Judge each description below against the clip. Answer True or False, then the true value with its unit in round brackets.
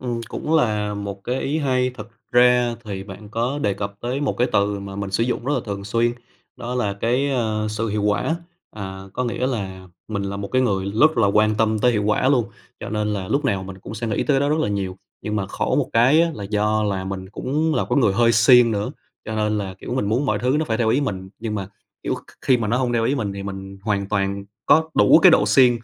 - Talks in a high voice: False (110 Hz)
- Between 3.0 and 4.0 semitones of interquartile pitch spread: True (3.7 semitones)